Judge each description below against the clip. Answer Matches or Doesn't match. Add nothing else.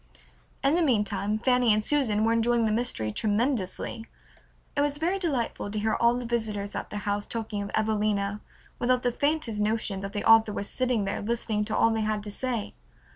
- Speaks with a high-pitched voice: Matches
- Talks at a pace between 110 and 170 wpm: Doesn't match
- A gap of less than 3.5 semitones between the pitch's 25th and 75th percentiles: Matches